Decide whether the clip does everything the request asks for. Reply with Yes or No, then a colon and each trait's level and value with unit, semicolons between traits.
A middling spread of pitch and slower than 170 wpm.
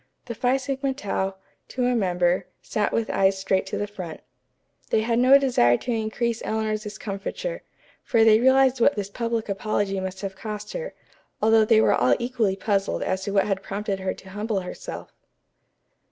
No: average, 3.5 semitones; average, 180 wpm